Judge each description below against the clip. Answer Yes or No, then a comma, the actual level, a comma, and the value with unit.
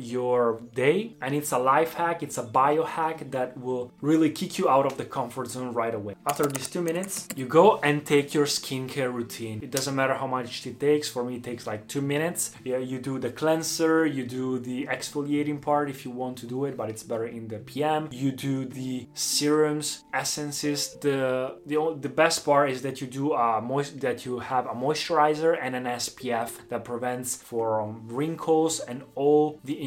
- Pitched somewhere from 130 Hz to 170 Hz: Yes, low, 135 Hz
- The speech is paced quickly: Yes, fast, 200 wpm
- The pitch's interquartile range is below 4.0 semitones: Yes, average, 3.1 semitones